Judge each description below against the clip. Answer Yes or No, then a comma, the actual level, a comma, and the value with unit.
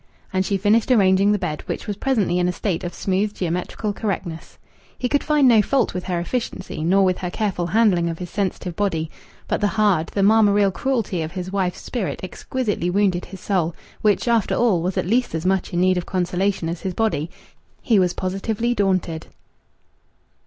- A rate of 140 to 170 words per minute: No, average, 195 wpm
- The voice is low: No, high, 190 Hz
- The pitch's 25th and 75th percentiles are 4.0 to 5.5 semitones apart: No, average, 3.0 semitones